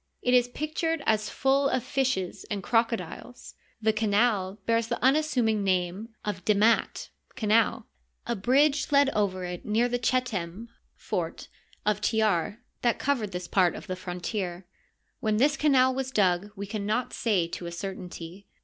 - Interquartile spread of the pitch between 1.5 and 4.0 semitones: No, average, 4.7 semitones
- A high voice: Yes, high, 215 Hz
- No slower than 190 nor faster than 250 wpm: No, average, 160 wpm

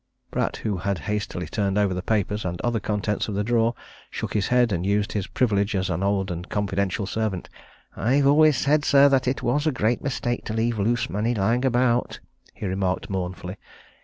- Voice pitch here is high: No, low, 105 Hz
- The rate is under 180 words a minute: No, average, 195 wpm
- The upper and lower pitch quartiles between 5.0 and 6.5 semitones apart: No, average, 3.8 semitones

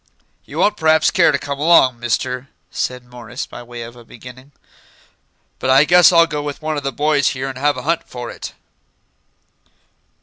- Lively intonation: No, average, 3.6 semitones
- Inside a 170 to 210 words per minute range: Yes, average, 190 wpm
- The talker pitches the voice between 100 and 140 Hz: Yes, low, 135 Hz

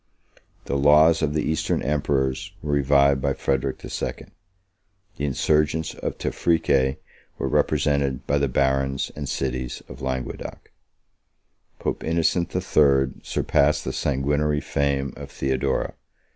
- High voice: No, very low, 70 Hz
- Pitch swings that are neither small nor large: No, narrow, 2.0 semitones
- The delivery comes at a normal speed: No, slow, 125 wpm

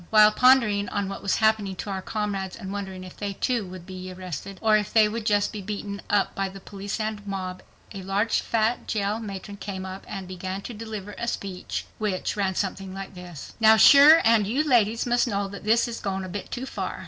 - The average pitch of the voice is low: No, high, 200 Hz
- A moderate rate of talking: No, fast, 220 wpm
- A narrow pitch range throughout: Yes, narrow, 2.3 semitones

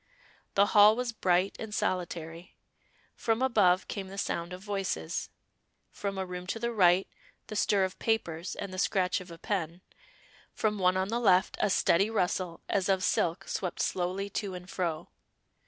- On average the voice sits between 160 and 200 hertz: Yes, high, 190 Hz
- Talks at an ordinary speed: Yes, average, 170 wpm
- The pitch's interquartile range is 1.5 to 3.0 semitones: Yes, narrow, 2.4 semitones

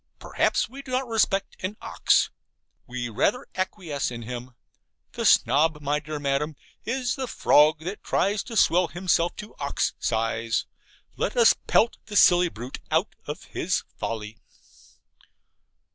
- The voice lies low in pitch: No, medium, 160 Hz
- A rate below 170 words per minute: Yes, average, 145 wpm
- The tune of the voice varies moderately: No, wide, 8.6 semitones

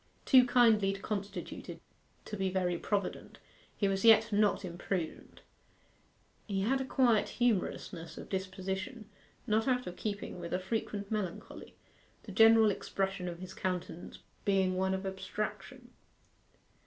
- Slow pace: Yes, slow, 130 wpm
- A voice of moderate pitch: No, high, 195 Hz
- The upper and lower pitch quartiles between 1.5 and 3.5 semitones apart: Yes, average, 2.8 semitones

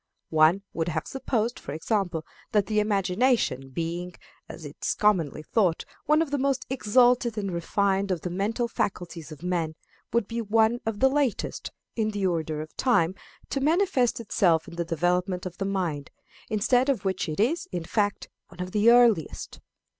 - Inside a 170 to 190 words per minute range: Yes, average, 175 wpm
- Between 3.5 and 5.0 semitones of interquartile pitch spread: No, wide, 5.5 semitones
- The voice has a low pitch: No, high, 195 Hz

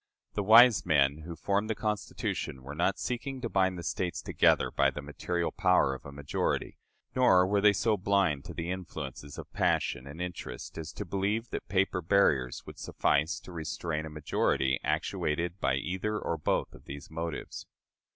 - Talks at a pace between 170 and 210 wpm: Yes, average, 180 wpm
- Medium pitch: No, very low, 85 Hz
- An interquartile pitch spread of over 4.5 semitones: Yes, average, 5.2 semitones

